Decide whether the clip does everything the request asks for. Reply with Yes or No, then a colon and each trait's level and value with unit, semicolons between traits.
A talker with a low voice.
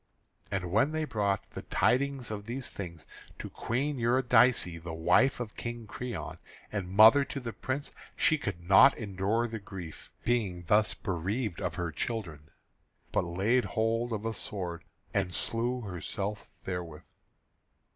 Yes: low, 105 Hz